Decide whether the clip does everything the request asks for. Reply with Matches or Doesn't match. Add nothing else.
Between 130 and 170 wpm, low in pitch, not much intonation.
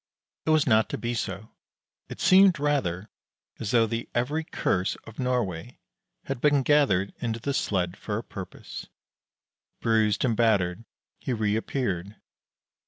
Doesn't match